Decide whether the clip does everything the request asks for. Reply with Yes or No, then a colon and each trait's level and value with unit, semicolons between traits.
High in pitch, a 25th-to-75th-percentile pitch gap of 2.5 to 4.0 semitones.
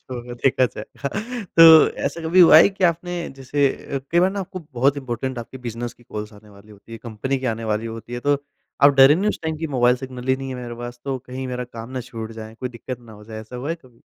No: low, 125 Hz; average, 3.5 semitones